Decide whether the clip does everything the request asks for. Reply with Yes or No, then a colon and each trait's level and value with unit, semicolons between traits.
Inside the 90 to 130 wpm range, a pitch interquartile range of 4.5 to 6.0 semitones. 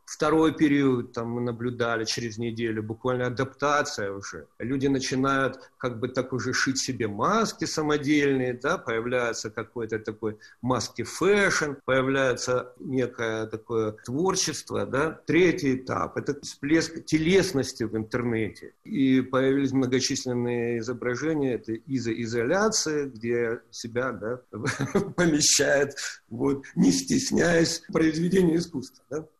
No: slow, 110 wpm; average, 3.7 semitones